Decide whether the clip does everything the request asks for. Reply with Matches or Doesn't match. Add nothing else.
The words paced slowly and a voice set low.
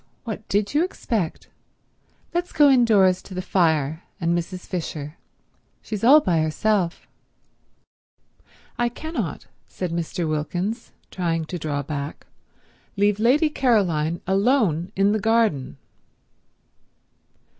Doesn't match